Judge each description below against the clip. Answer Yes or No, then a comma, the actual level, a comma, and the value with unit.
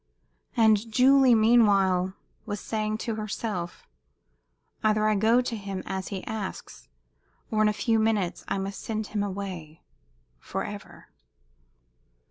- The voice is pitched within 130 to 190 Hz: No, high, 215 Hz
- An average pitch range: No, narrow, 2.3 semitones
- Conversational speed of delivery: No, slow, 125 wpm